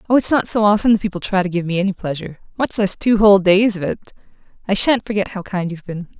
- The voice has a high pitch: Yes, high, 195 Hz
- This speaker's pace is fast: Yes, fast, 250 wpm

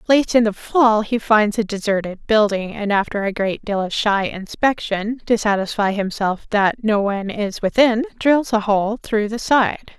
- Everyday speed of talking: Yes, average, 185 wpm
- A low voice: No, high, 215 Hz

